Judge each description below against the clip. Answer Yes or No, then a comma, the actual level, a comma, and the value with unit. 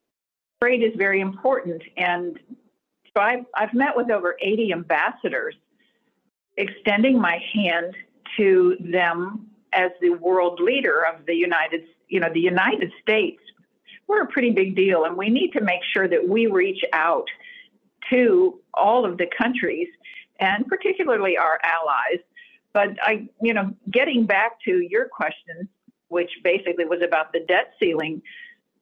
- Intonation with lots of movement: Yes, wide, 7.0 semitones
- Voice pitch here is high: Yes, high, 210 Hz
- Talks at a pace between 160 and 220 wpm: No, average, 145 wpm